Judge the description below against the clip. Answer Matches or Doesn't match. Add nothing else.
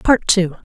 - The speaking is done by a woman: Matches